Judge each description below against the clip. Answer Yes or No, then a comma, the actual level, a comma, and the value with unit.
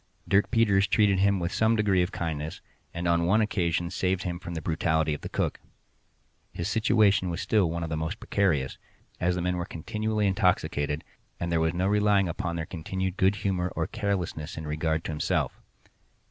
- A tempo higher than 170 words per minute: Yes, average, 190 wpm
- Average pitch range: Yes, average, 3.3 semitones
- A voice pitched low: Yes, very low, 90 Hz